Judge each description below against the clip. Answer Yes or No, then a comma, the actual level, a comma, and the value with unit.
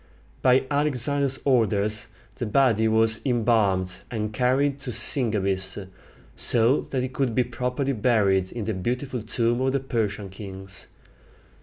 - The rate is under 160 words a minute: Yes, slow, 135 wpm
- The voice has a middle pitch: No, low, 115 Hz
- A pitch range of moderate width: Yes, average, 3.9 semitones